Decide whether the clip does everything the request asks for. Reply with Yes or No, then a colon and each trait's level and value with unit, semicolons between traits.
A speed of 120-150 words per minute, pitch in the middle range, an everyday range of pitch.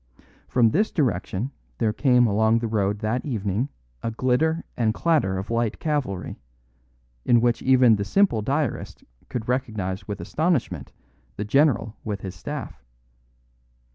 No: average, 140 wpm; low, 115 Hz; average, 4.4 semitones